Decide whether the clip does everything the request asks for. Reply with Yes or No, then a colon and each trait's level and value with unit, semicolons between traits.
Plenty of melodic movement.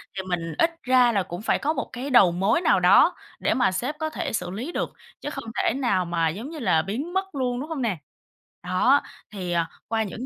Yes: wide, 7.2 semitones